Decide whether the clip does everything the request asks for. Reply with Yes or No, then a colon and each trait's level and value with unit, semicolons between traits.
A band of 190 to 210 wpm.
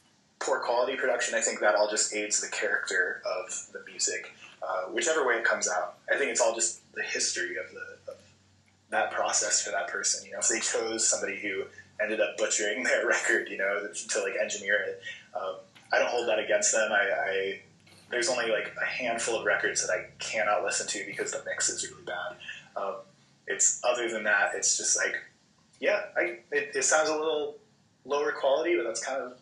Yes: fast, 205 wpm